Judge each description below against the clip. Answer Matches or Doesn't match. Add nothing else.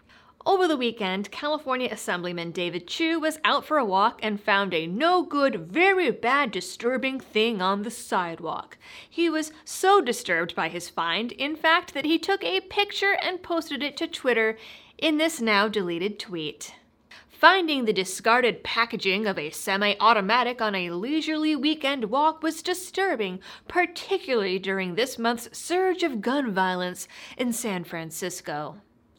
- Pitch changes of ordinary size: Doesn't match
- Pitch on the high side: Matches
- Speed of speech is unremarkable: Matches